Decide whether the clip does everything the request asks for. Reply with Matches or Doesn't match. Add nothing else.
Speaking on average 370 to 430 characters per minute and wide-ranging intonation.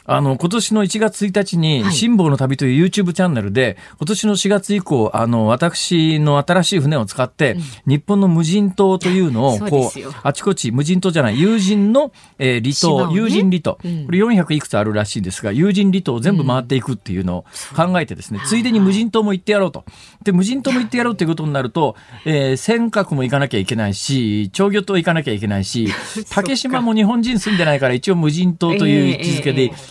Matches